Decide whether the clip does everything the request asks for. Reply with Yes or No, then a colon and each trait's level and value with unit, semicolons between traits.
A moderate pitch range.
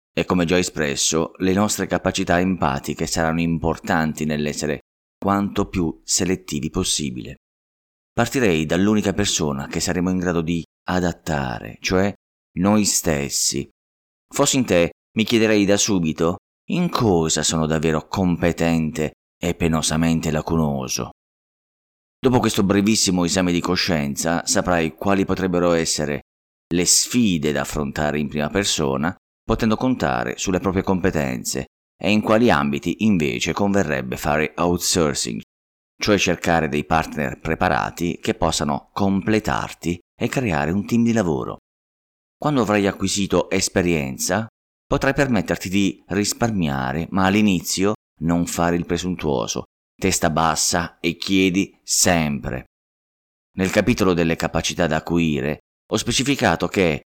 Yes: average, 4.2 semitones